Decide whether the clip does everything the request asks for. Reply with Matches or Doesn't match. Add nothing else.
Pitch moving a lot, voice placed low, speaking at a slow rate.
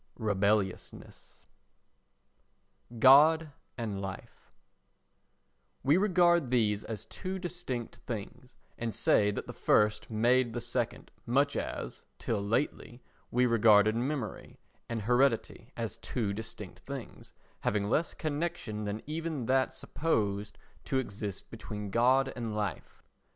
Doesn't match